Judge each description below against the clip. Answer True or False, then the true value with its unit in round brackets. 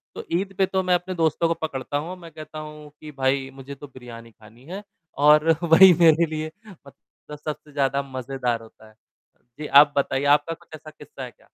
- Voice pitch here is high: False (150 Hz)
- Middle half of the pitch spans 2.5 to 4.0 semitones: True (3.4 semitones)